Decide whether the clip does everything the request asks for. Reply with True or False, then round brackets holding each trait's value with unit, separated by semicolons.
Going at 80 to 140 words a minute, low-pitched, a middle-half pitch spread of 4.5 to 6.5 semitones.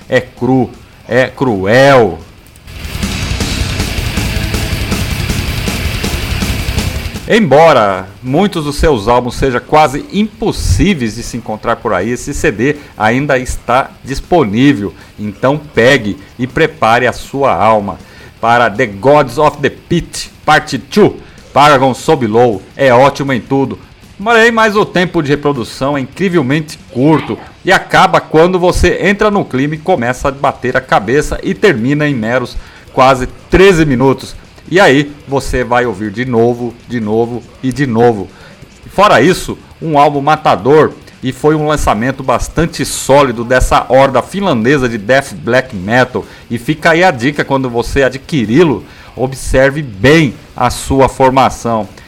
True (130 wpm; 125 Hz; 5.0 semitones)